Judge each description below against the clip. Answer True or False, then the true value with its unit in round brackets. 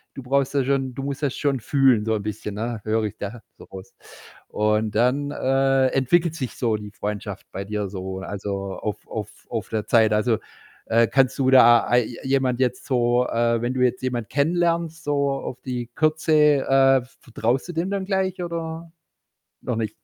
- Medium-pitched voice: False (125 Hz)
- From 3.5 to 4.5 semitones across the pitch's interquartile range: True (4.2 semitones)